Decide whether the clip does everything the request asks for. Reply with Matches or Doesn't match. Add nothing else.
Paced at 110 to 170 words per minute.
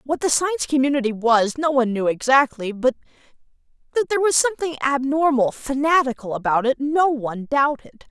Matches